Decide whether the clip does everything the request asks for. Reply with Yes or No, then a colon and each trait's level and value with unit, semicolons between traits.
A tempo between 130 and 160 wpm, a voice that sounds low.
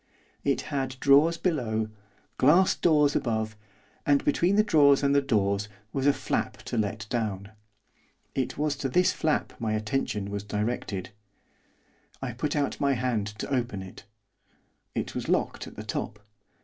Yes: average, 155 wpm; low, 130 Hz